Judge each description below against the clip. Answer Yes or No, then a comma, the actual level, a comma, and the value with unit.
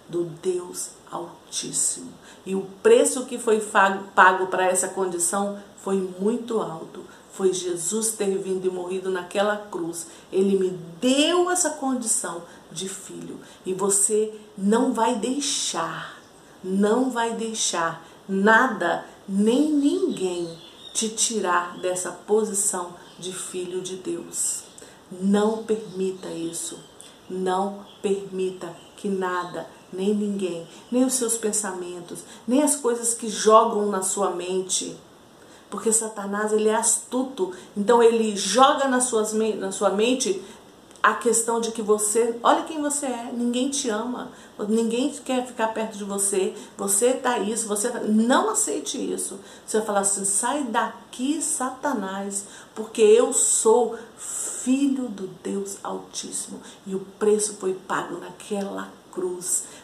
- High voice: Yes, high, 210 Hz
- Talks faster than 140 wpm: No, average, 130 wpm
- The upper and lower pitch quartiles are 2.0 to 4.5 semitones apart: Yes, average, 3.7 semitones